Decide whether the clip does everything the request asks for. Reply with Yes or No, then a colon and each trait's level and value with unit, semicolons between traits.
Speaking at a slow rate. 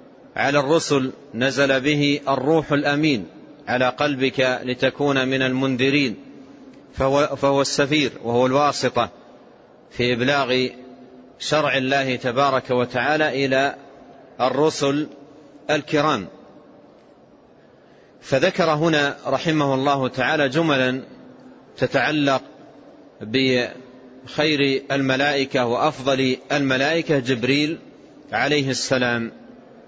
No: average, 80 wpm